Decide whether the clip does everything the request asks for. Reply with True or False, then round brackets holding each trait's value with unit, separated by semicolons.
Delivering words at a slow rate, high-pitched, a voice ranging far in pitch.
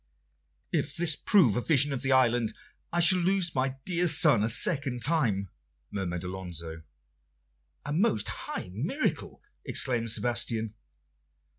False (130 wpm; 130 Hz; 7.4 semitones)